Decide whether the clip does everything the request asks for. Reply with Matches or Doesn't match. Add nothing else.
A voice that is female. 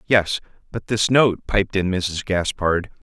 Doesn't match